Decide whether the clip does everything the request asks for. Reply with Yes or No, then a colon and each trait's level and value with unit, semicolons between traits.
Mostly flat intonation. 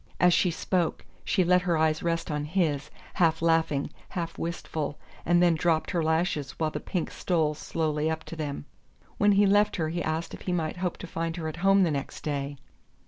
Yes: narrow, 2.3 semitones